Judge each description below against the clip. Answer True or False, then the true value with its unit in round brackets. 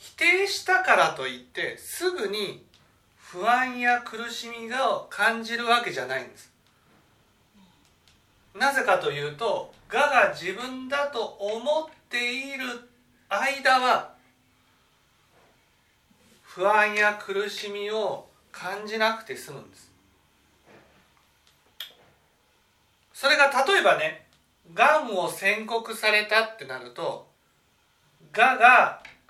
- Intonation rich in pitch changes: False (4.8 semitones)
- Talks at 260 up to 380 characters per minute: False (190 characters per minute)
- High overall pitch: True (235 Hz)